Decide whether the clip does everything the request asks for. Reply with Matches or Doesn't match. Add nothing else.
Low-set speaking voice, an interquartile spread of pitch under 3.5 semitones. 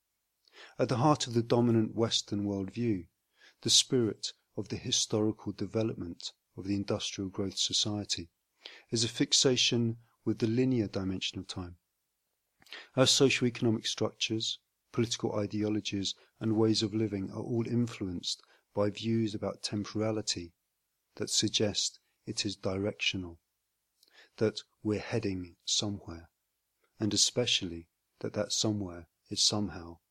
Matches